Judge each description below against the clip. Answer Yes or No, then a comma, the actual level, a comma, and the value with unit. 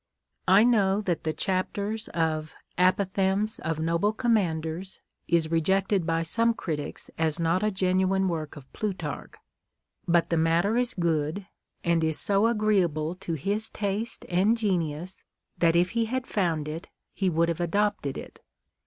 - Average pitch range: Yes, average, 3.8 semitones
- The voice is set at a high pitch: No, medium, 180 Hz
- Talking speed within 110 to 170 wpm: Yes, average, 160 wpm